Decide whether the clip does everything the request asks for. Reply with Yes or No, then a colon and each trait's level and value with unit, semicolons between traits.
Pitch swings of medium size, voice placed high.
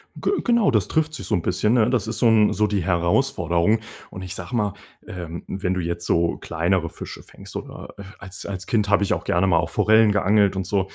No: average, 3.5 semitones; low, 100 Hz